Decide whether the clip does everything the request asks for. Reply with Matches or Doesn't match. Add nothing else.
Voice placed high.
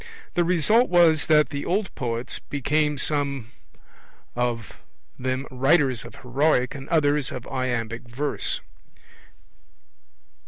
Doesn't match